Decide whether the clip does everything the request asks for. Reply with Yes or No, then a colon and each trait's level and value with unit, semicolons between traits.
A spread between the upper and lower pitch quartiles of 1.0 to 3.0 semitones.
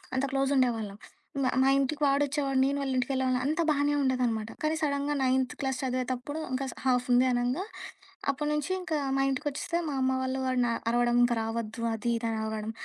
Yes: narrow, 2.5 semitones